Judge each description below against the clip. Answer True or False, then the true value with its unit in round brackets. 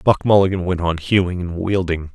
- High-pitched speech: False (90 Hz)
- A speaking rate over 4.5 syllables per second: True (5.4 syllables/s)